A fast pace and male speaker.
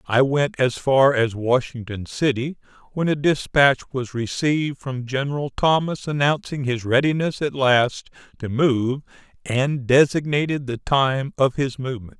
No: average, 145 wpm; male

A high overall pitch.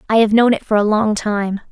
Yes: high, 215 Hz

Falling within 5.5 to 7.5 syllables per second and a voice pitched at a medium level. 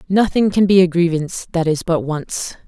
No: 5.1 syllables/s; medium, 175 Hz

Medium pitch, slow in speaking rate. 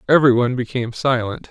No: low, 125 Hz; slow, 120 wpm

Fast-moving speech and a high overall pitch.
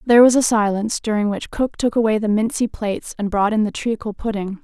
Yes: fast, 235 wpm; high, 215 Hz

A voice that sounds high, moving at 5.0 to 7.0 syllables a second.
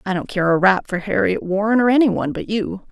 Yes: high, 200 Hz; 5.8 syllables/s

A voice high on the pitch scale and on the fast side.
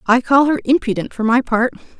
Yes: high, 245 Hz; fast, 210 wpm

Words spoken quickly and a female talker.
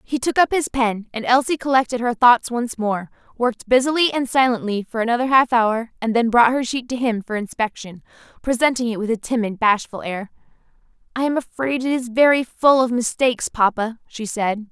No: average, 195 wpm; female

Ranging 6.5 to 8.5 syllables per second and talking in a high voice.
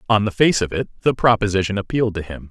No: 6.9 syllables/s; low, 105 Hz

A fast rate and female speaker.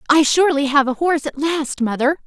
Yes: fast, 210 wpm; female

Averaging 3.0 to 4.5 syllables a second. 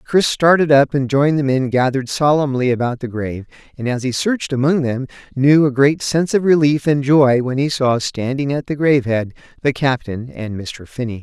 No: 5.4 syllables/s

